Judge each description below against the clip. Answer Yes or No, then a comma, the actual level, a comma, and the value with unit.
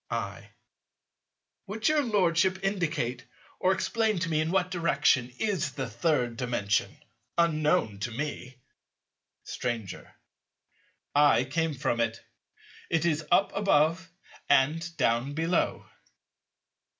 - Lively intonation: Yes, wide, 6.1 semitones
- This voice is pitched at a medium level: Yes, medium, 155 Hz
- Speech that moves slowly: Yes, slow, 110 wpm